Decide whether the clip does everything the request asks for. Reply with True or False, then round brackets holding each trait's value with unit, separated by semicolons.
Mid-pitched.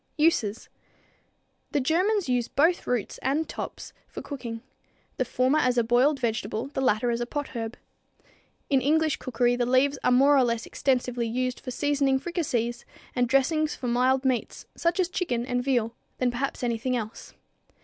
False (255 Hz)